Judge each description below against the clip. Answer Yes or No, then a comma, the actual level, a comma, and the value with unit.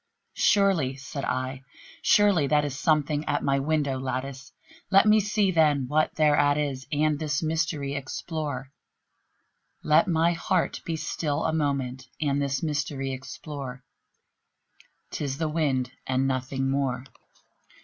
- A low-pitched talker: No, medium, 145 Hz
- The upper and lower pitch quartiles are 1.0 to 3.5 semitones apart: Yes, average, 2.8 semitones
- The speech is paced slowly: Yes, slow, 130 wpm